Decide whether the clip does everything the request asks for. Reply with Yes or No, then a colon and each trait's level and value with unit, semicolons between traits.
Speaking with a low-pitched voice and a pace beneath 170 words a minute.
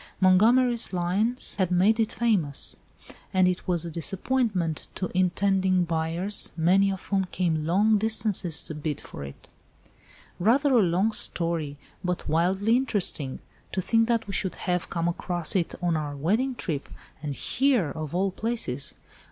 No: medium, 185 Hz; average, 150 wpm